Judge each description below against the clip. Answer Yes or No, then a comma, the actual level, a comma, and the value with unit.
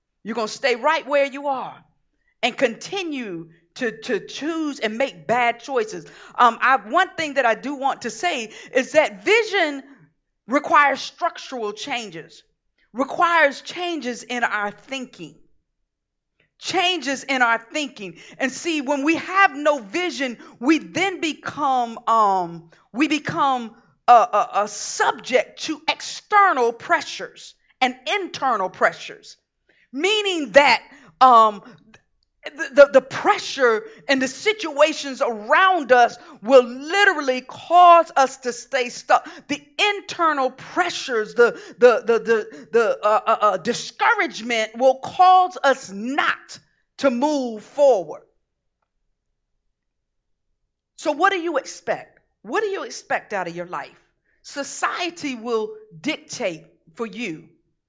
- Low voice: No, very high, 275 Hz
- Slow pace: Yes, slow, 125 wpm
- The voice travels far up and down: Yes, wide, 6.2 semitones